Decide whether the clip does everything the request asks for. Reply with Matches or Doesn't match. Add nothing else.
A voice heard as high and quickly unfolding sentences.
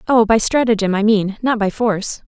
Matches